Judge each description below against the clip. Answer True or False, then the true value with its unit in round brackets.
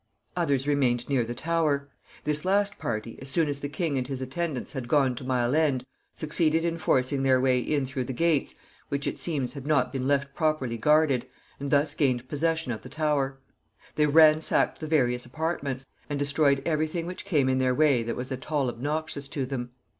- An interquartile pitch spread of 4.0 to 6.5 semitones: False (3.2 semitones)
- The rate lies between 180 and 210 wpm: True (200 wpm)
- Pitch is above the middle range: False (140 Hz)